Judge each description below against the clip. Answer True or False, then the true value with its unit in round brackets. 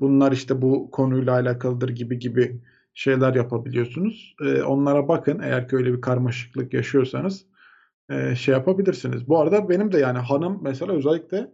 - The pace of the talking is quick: True (145 wpm)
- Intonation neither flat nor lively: True (3.6 semitones)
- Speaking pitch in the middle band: False (130 Hz)